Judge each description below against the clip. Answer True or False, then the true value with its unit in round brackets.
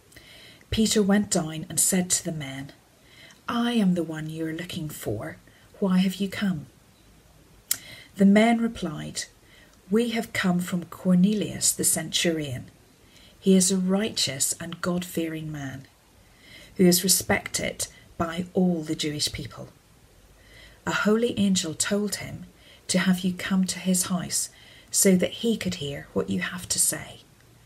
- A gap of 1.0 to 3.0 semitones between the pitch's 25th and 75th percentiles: False (4.1 semitones)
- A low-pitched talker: False (175 Hz)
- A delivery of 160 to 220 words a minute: False (150 wpm)